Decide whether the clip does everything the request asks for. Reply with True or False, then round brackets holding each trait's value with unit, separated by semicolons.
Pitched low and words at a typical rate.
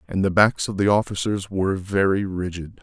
True (95 Hz; 190 wpm)